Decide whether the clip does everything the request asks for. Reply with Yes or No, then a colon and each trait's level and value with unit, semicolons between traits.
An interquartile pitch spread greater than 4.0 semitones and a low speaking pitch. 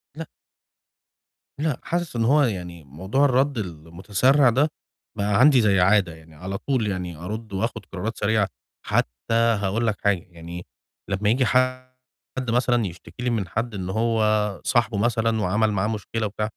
Yes: average, 4.5 semitones; low, 110 Hz